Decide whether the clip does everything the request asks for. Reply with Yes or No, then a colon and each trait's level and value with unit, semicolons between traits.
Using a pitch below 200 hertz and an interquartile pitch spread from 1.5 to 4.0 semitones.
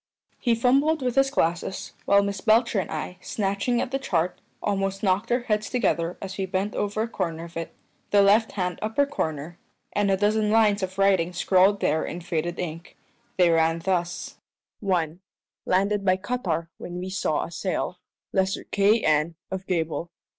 Yes: high, 190 Hz; average, 3.5 semitones